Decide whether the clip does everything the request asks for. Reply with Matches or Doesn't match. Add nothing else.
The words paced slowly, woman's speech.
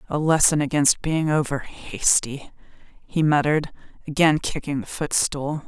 Matches